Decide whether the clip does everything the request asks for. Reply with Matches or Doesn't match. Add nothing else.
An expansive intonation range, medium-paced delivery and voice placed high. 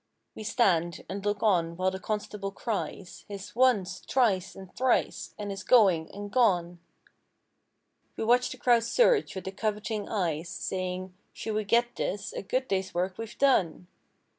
Doesn't match